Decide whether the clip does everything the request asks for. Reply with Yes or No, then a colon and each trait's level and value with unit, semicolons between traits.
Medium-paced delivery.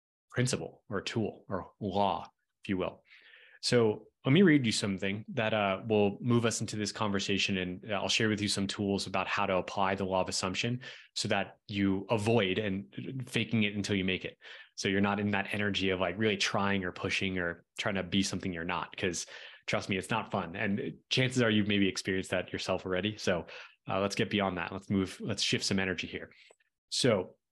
No: fast, 210 wpm